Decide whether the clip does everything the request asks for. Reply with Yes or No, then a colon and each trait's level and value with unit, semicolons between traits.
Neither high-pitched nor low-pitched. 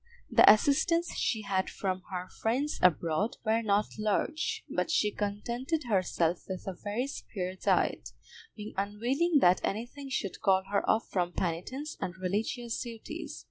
No: high, 210 Hz